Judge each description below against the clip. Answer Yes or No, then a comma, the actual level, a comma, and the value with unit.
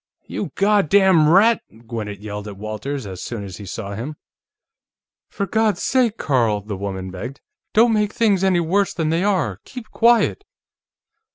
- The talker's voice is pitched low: No, medium, 155 Hz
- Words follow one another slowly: No, average, 160 wpm